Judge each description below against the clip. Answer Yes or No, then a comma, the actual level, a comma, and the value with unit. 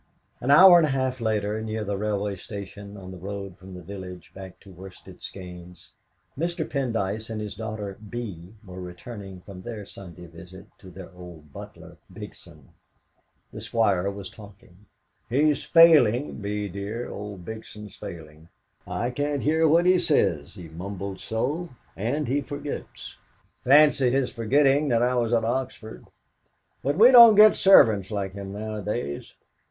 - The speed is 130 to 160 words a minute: Yes, average, 155 wpm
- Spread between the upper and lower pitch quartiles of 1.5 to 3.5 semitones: No, wide, 5.4 semitones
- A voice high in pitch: No, low, 105 Hz